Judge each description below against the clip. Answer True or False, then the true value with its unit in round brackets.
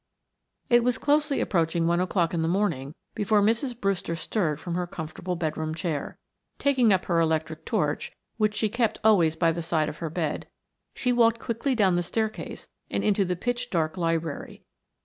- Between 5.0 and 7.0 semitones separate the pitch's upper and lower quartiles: True (5.3 semitones)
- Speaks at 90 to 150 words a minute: False (180 wpm)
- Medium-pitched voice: True (180 Hz)